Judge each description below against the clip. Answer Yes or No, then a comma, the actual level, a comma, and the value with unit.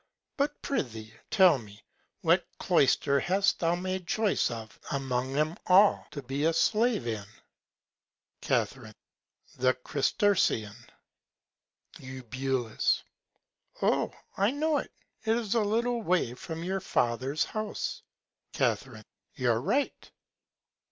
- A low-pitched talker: No, medium, 160 Hz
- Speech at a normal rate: No, slow, 110 wpm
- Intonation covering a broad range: Yes, wide, 8.5 semitones